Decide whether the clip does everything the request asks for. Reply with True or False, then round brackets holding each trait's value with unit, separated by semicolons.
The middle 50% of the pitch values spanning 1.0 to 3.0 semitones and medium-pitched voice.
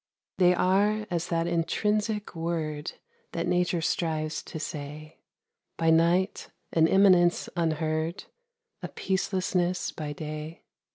True (2.7 semitones; 170 Hz)